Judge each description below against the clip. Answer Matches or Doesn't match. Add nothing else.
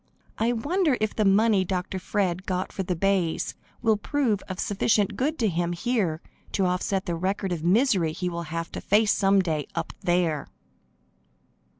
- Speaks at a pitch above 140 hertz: Matches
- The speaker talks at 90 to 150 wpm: Doesn't match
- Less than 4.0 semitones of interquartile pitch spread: Matches